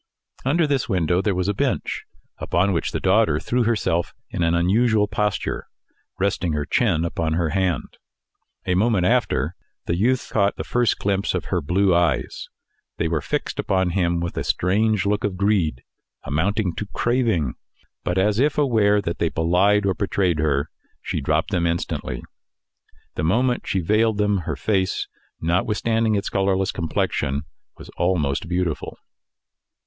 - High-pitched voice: No, very low, 95 Hz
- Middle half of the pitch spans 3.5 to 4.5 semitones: Yes, average, 3.8 semitones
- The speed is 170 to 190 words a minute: No, average, 155 wpm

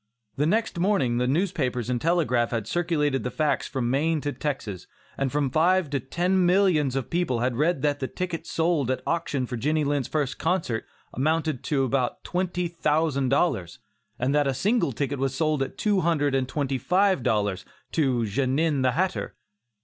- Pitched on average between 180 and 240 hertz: No, medium, 145 Hz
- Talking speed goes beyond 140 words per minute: Yes, average, 180 wpm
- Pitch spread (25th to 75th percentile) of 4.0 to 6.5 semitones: Yes, average, 4.5 semitones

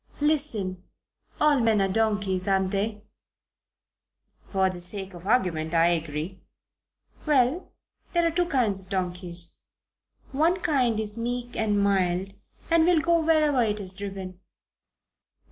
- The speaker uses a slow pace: Yes, slow, 130 wpm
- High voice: Yes, high, 205 Hz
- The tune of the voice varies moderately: No, wide, 6.4 semitones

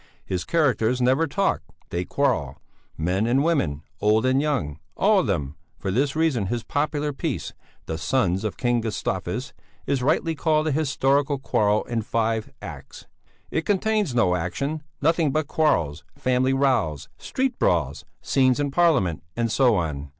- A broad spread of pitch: Yes, wide, 7.2 semitones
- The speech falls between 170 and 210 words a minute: No, average, 155 wpm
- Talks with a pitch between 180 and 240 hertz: No, low, 130 Hz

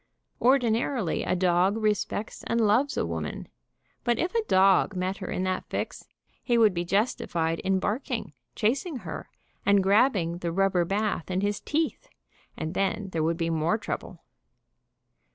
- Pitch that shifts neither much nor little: Yes, average, 4.1 semitones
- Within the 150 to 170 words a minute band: Yes, average, 155 wpm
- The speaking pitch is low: No, high, 195 Hz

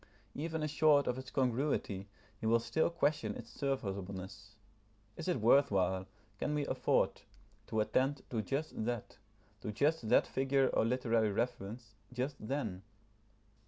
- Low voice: Yes, low, 125 Hz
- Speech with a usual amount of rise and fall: Yes, average, 4.9 semitones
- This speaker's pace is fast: No, average, 140 wpm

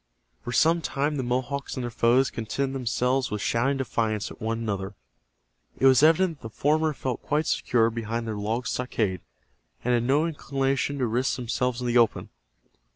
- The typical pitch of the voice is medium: No, low, 125 Hz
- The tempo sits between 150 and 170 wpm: No, average, 180 wpm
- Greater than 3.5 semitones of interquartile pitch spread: No, average, 3.2 semitones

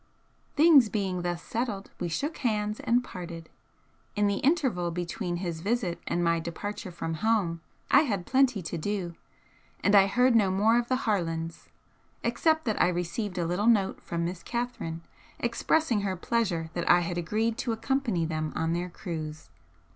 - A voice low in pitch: No, high, 195 Hz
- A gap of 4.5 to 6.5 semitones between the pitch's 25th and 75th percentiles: Yes, average, 5.2 semitones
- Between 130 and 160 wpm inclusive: No, average, 170 wpm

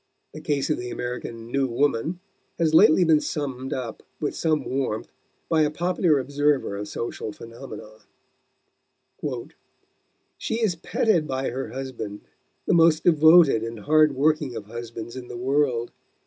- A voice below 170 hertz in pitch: Yes, medium, 140 Hz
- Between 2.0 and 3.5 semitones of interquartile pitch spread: No, average, 4.6 semitones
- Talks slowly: No, average, 145 wpm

